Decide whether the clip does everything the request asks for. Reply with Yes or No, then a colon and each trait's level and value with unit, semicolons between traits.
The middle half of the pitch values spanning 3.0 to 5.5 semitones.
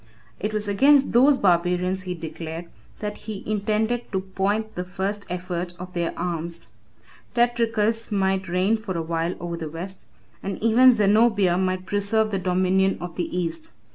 Yes: average, 3.4 semitones